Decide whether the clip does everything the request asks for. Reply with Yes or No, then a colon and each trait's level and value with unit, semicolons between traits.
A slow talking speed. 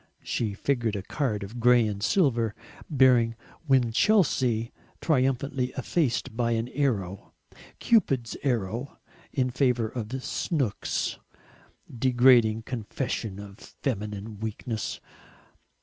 Yes: slow, 100 wpm